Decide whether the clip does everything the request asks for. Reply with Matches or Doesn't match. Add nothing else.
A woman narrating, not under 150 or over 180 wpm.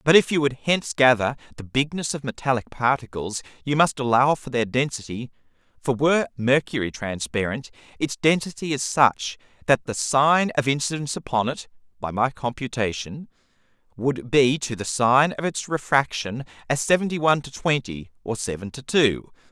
Doesn't match